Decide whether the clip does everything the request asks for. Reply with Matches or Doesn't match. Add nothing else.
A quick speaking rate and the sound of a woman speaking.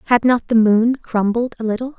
Matches